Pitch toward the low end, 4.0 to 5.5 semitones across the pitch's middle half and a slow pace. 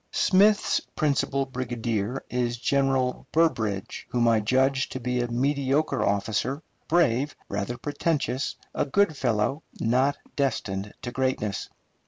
No: low, 130 Hz; average, 3.3 semitones; slow, 120 wpm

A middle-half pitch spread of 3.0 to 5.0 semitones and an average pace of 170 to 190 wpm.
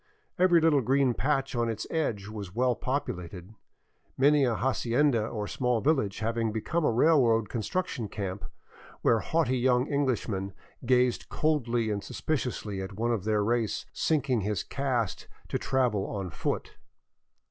No: average, 4.3 semitones; average, 145 wpm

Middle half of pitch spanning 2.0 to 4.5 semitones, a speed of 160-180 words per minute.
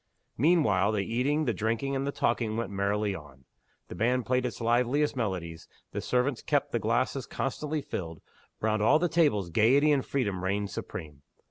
No: average, 5.3 semitones; average, 170 wpm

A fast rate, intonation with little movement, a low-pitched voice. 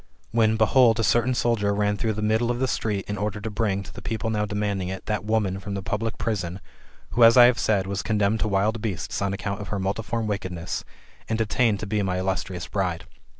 Yes: fast, 230 wpm; narrow, 2.3 semitones; low, 105 Hz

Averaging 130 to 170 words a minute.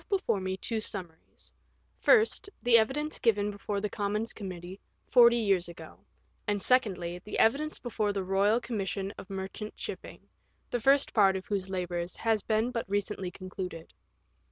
Yes: average, 155 wpm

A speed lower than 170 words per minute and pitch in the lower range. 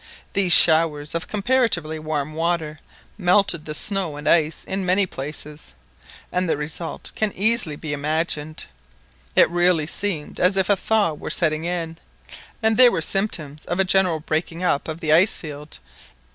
No: average, 160 wpm; medium, 165 Hz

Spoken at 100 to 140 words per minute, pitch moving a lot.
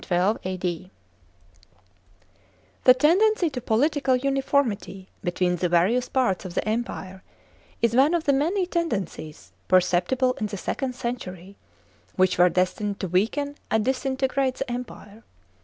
Yes: slow, 135 wpm; wide, 6.7 semitones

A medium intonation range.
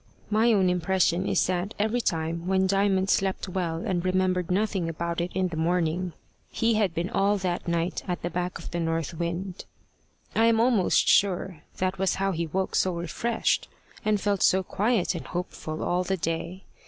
No: narrow, 2.3 semitones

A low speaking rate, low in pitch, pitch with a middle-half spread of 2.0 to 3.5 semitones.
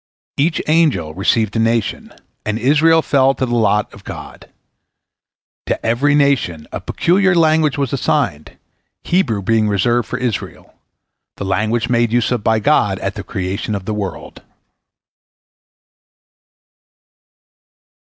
No: slow, 125 wpm; low, 120 Hz; average, 5.2 semitones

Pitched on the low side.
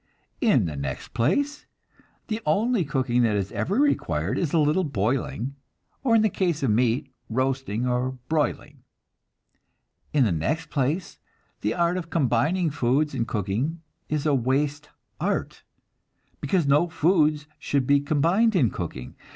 No: medium, 145 Hz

